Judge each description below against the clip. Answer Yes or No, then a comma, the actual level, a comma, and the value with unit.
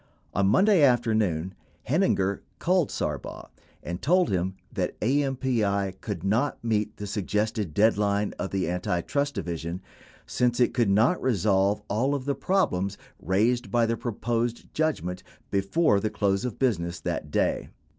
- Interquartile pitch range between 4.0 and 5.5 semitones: Yes, average, 4.6 semitones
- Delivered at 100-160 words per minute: Yes, average, 140 wpm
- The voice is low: Yes, low, 105 Hz